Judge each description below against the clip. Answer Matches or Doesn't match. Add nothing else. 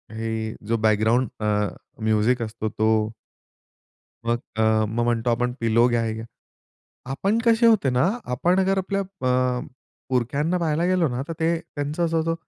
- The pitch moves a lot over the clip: Matches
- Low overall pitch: Matches